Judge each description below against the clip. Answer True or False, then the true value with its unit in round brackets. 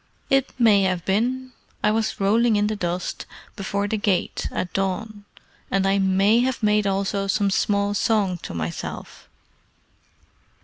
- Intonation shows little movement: True (2.1 semitones)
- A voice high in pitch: True (205 Hz)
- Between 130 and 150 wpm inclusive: True (145 wpm)